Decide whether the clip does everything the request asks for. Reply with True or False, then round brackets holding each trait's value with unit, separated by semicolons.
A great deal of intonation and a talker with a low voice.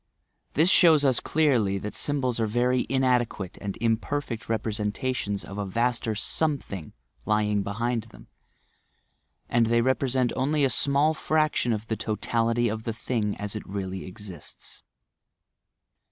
False (3.7 semitones; 115 Hz)